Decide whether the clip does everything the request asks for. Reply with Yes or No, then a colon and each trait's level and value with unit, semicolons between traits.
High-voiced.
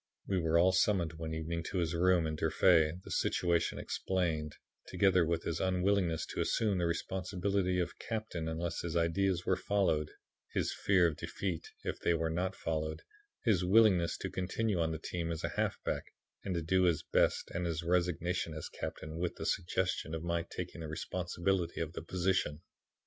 No: very low, 85 Hz